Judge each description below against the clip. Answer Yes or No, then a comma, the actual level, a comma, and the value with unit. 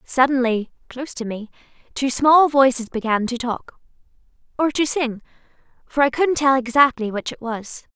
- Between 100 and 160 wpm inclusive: Yes, average, 150 wpm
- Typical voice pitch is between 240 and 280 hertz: Yes, very high, 255 Hz